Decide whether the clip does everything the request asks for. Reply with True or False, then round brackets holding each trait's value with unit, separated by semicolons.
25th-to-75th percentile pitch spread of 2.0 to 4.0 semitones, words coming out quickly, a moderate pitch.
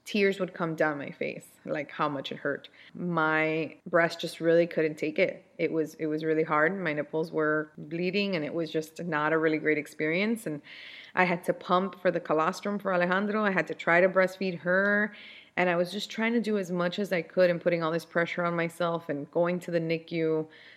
True (2.7 semitones; 225 wpm; 170 Hz)